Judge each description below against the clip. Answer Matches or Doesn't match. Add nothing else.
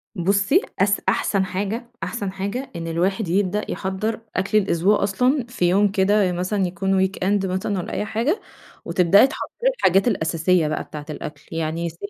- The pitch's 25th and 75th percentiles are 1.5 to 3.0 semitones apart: Matches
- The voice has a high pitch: Matches